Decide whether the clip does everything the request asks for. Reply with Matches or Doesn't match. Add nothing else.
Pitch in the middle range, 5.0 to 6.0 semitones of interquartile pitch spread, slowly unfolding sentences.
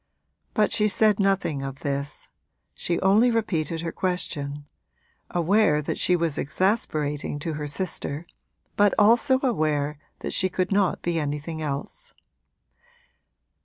Matches